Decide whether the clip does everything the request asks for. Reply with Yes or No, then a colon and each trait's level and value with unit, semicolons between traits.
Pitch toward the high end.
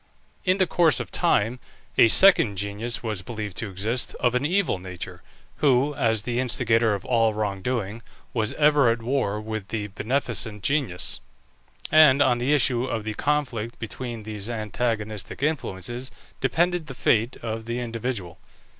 No: low, 115 Hz